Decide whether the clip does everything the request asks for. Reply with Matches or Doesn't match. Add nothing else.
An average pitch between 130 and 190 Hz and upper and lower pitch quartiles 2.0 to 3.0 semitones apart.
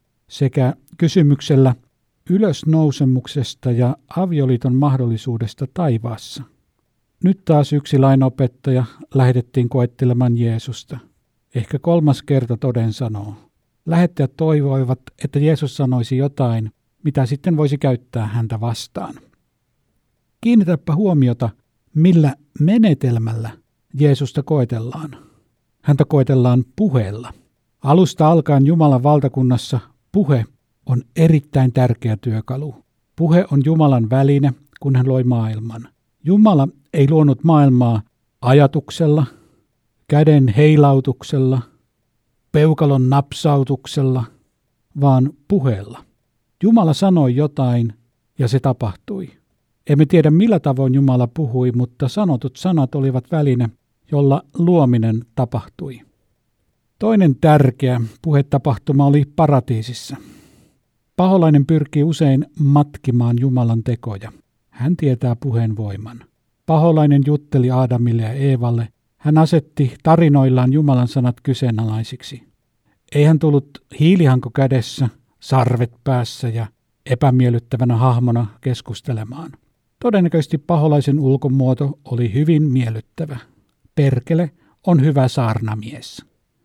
Doesn't match